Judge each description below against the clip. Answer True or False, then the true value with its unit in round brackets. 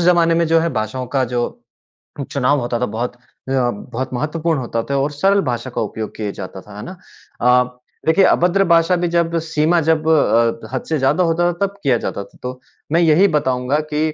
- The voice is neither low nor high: True (145 Hz)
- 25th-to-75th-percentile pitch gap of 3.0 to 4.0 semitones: False (5.3 semitones)